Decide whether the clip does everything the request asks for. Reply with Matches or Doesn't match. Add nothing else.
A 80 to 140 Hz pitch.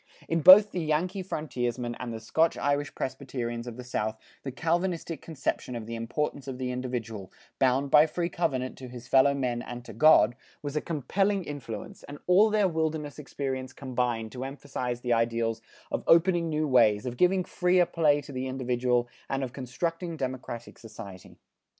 Matches